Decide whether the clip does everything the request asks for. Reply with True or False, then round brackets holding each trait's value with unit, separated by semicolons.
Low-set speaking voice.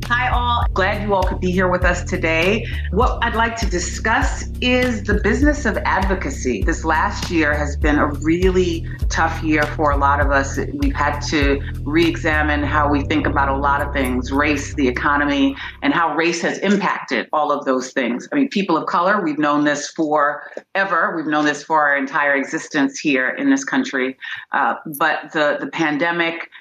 False (150 Hz)